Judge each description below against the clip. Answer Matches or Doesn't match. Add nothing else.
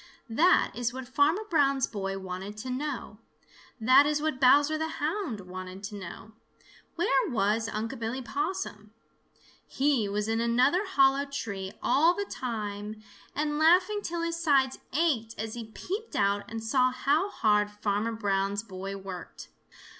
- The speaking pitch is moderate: Doesn't match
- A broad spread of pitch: Matches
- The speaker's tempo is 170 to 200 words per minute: Doesn't match